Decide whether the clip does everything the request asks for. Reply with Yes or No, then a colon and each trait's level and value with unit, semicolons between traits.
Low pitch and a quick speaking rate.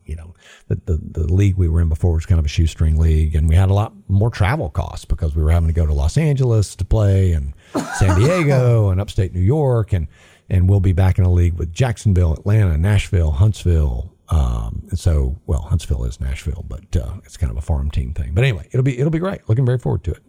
Yes: very low, 90 Hz; fast, 245 wpm